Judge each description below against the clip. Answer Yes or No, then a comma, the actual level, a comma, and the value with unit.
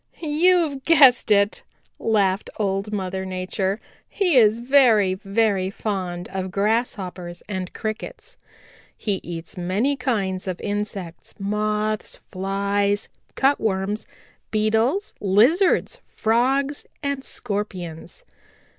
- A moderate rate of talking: No, slow, 95 wpm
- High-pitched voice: Yes, high, 210 Hz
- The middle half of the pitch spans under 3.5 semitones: No, average, 4.4 semitones